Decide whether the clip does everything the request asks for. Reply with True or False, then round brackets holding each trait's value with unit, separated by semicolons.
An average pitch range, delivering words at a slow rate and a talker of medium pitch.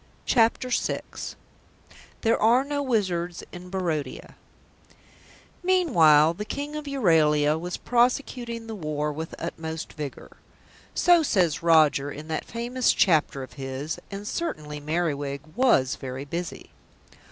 False (7.8 semitones; 120 wpm; 170 Hz)